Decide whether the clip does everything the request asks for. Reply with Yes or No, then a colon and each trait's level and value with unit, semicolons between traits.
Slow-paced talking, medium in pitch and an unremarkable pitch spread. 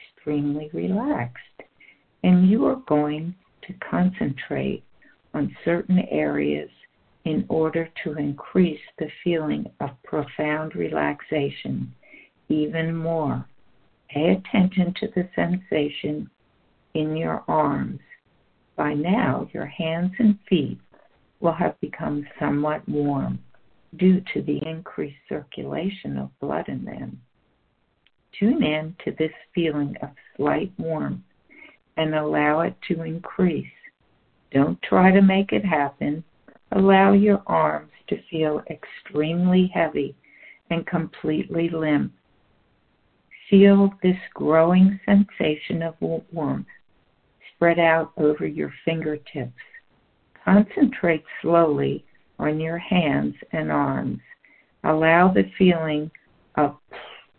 Yes: slow, 105 wpm; medium, 160 Hz; average, 3.7 semitones